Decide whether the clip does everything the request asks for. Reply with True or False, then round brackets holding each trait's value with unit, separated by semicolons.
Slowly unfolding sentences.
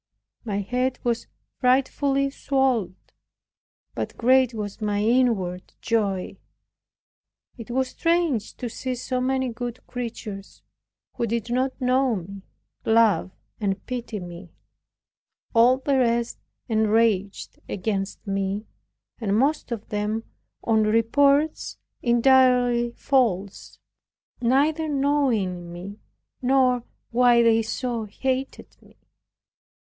True (105 wpm)